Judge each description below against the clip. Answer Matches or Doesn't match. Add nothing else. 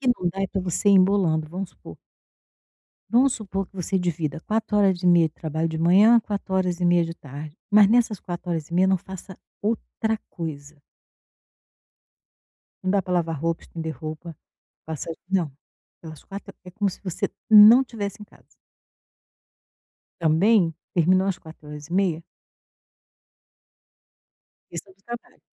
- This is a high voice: Doesn't match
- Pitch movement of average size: Matches